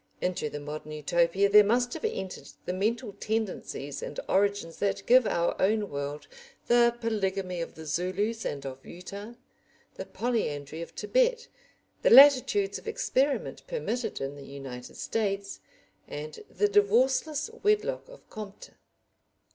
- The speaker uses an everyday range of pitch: No, wide, 6.6 semitones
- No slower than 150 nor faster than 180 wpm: No, average, 140 wpm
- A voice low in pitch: No, high, 200 Hz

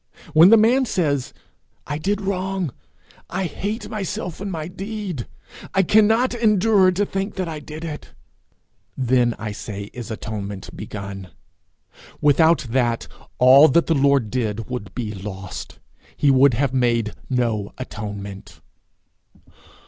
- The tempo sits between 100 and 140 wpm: Yes, slow, 135 wpm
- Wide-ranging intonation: Yes, wide, 9.0 semitones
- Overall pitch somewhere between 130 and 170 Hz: Yes, medium, 140 Hz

